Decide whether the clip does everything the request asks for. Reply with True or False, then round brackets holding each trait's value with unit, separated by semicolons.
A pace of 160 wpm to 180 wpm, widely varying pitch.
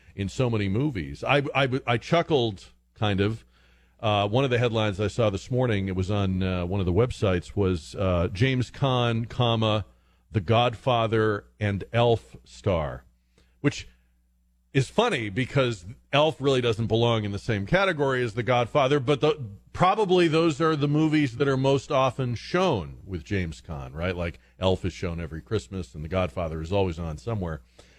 True (175 wpm; 6.2 semitones)